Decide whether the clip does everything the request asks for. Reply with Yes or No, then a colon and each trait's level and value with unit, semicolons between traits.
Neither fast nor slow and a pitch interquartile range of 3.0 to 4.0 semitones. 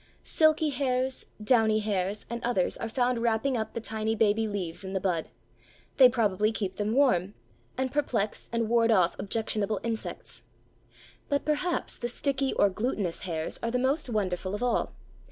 Yes: average, 165 wpm; average, 3.7 semitones